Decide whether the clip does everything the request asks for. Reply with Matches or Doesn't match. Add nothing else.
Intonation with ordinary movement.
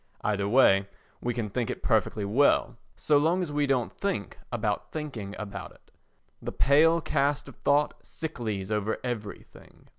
Doesn't match